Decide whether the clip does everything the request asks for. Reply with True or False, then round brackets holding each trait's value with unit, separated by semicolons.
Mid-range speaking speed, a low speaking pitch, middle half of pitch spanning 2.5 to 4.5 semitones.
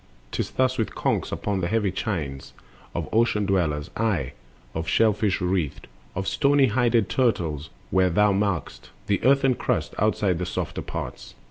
True (155 wpm; 100 Hz; 4.2 semitones)